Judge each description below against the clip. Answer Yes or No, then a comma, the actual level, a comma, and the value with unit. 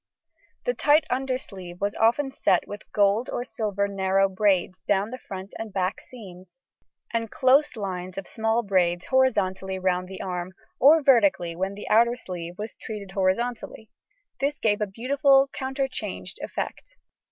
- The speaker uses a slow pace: No, average, 150 wpm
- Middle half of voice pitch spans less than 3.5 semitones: No, average, 4.8 semitones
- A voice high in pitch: Yes, high, 205 Hz